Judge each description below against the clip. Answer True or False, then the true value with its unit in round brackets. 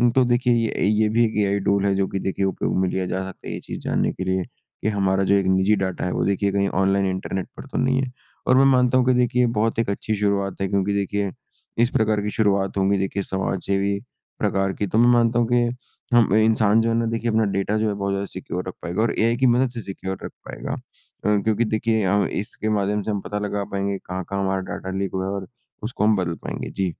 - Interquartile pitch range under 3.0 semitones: True (2.5 semitones)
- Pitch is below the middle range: True (100 Hz)